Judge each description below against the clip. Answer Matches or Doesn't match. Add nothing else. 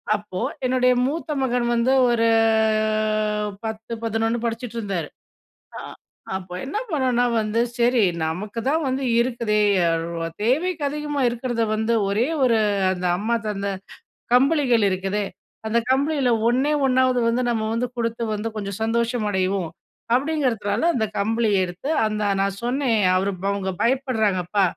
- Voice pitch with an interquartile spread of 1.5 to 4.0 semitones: Matches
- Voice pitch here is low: Doesn't match